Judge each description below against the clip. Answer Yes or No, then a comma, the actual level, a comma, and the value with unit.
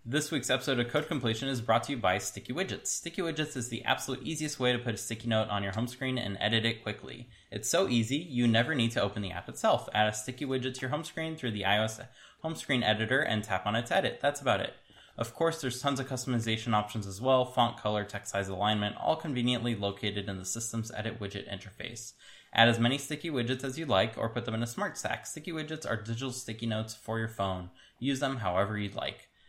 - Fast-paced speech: Yes, fast, 240 wpm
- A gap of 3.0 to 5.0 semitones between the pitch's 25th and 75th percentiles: Yes, average, 3.7 semitones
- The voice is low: Yes, low, 115 Hz